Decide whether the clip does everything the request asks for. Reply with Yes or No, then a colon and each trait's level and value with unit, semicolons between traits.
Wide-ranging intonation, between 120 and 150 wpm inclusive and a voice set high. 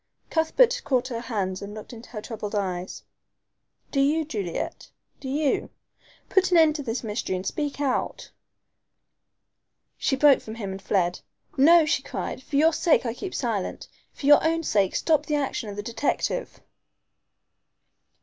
No: wide, 6.6 semitones; average, 160 wpm; very high, 260 Hz